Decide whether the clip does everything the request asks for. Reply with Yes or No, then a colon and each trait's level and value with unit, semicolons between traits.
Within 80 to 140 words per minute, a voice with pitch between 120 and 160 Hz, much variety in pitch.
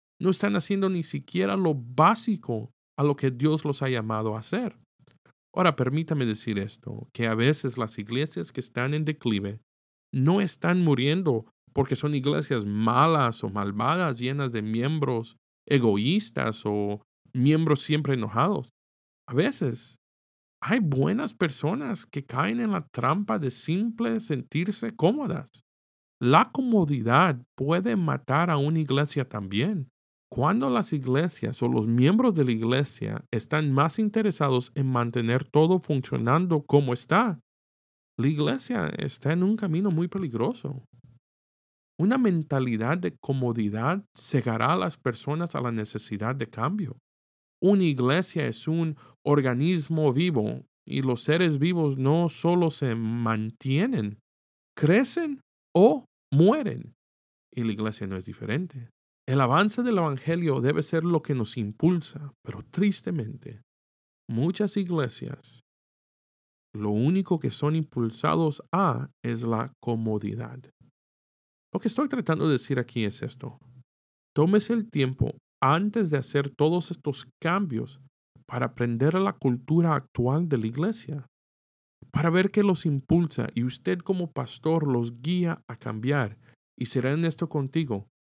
Yes: average, 135 wpm; medium, 140 Hz; wide, 6.1 semitones